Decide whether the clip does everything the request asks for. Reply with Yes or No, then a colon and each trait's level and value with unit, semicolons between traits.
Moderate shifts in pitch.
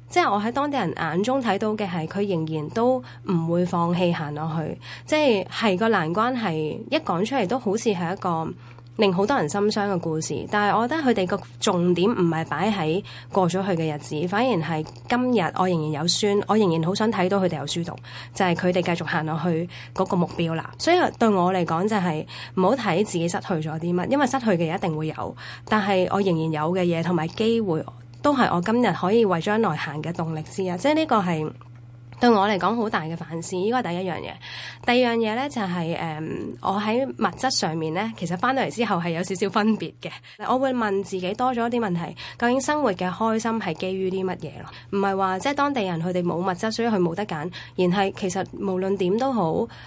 Yes: average, 4.7 semitones